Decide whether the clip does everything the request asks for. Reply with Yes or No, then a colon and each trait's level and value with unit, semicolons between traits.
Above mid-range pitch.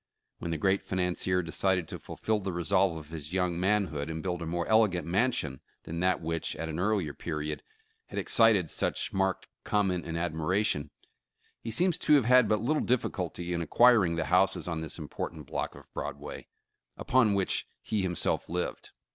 No: very low, 90 Hz